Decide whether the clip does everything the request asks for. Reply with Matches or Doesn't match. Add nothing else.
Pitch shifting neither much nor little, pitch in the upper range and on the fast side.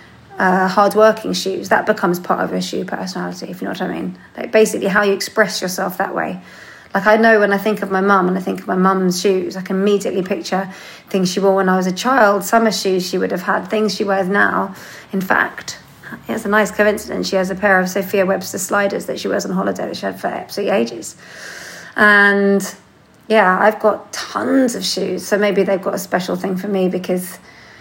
Doesn't match